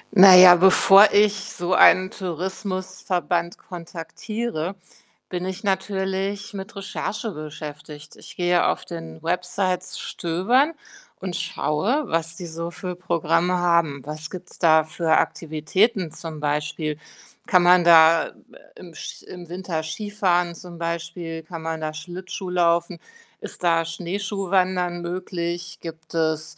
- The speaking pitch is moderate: Yes, medium, 175 Hz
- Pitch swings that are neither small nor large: No, narrow, 2.3 semitones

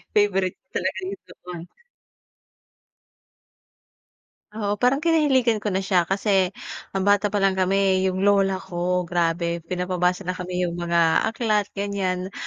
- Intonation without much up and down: Yes, narrow, 2.2 semitones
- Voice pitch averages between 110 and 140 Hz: No, high, 190 Hz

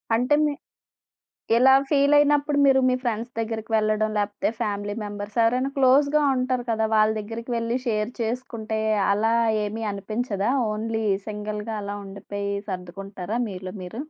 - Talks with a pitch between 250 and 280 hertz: No, high, 220 Hz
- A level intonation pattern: No, average, 3.4 semitones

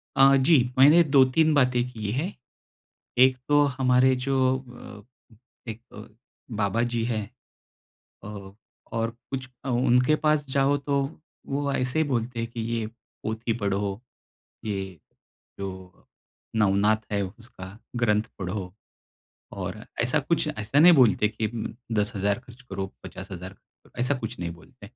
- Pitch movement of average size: Yes, average, 4.2 semitones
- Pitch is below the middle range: Yes, low, 115 Hz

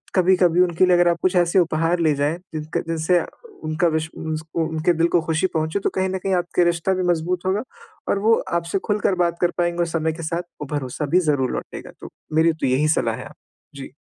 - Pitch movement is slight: Yes, narrow, 2.3 semitones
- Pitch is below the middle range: No, medium, 170 Hz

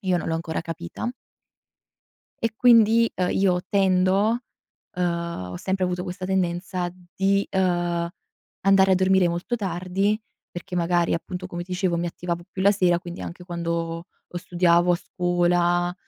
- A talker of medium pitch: Yes, medium, 180 Hz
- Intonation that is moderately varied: No, narrow, 1.7 semitones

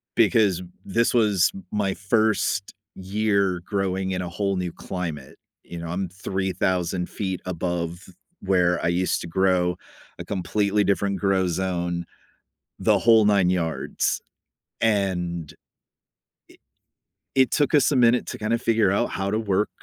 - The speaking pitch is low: Yes, very low, 95 Hz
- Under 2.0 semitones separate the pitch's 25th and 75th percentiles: No, average, 2.8 semitones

